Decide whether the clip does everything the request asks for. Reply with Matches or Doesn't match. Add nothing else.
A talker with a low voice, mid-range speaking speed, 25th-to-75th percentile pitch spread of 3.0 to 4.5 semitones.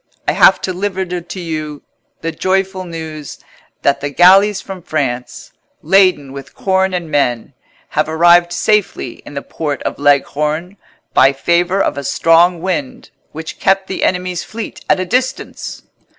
Doesn't match